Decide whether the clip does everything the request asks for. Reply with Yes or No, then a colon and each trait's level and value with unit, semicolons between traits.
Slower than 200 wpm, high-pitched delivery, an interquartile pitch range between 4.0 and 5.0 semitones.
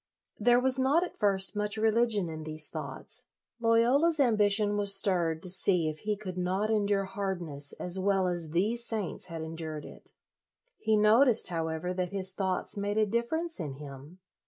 Yes: average, 180 wpm; high, 195 Hz; average, 4.4 semitones